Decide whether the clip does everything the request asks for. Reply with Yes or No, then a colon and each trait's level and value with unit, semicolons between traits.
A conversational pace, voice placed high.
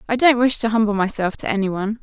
No: fast, 265 wpm; high, 220 Hz